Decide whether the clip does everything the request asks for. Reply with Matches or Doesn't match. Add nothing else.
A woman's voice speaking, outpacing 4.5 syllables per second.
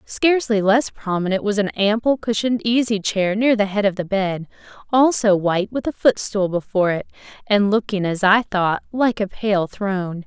Matches